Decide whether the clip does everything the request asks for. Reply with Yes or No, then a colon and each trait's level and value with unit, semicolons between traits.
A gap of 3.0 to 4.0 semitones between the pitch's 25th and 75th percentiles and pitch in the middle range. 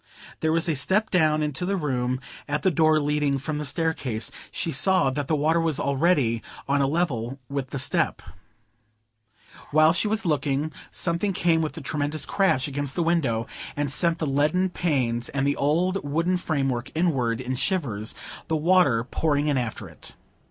Yes: average, 3.7 semitones; medium, 150 Hz